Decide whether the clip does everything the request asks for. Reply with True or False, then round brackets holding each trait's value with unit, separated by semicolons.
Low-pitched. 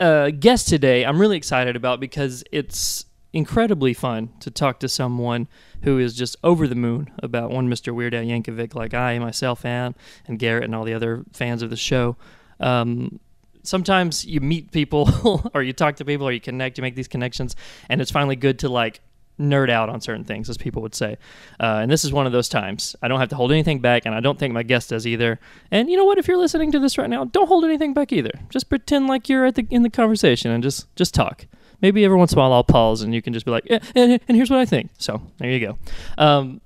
True (130 Hz)